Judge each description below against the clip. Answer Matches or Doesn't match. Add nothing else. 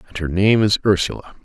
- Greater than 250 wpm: Doesn't match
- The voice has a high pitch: Doesn't match